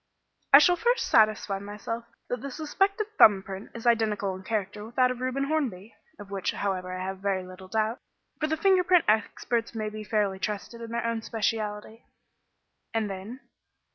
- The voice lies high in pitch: Yes, high, 220 Hz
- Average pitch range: Yes, average, 3.8 semitones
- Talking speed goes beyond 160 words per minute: Yes, average, 180 wpm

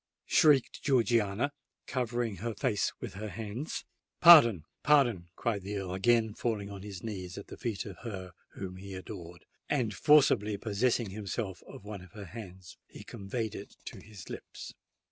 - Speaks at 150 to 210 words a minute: Yes, average, 160 wpm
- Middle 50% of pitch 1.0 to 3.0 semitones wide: No, average, 3.6 semitones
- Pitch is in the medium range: No, low, 105 Hz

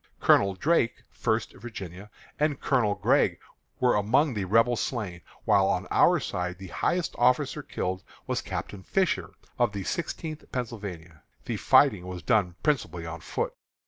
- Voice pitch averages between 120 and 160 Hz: No, low, 105 Hz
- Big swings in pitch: Yes, wide, 5.7 semitones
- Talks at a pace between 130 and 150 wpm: Yes, average, 145 wpm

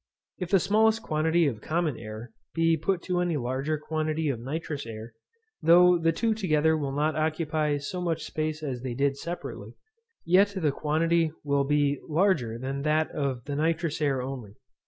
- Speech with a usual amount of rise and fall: Yes, average, 3.3 semitones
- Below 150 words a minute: No, average, 175 wpm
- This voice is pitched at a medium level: Yes, medium, 155 Hz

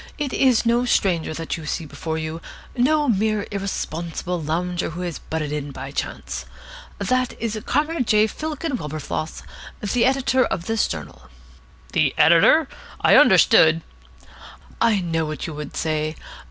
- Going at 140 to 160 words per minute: Yes, average, 150 wpm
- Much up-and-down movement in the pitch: Yes, wide, 7.0 semitones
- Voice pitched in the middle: Yes, medium, 180 Hz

